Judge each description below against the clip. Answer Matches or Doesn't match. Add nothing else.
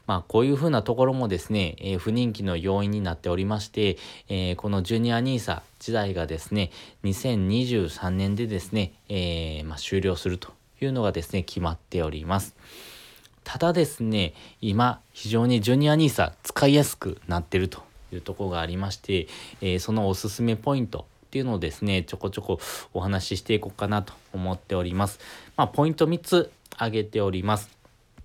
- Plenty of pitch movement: Doesn't match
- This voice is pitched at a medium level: Doesn't match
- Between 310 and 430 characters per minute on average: Matches